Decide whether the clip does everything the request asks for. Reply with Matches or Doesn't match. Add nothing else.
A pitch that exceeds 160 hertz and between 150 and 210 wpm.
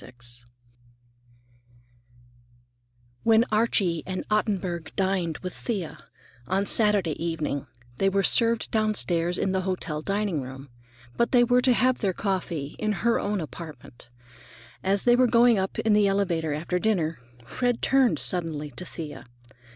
Doesn't match